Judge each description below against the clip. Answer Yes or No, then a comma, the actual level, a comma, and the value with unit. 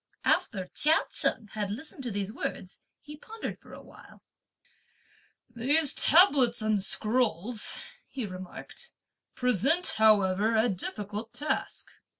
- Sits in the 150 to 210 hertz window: No, high, 225 Hz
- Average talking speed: No, slow, 120 wpm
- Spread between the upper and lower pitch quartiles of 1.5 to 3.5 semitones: No, average, 5.2 semitones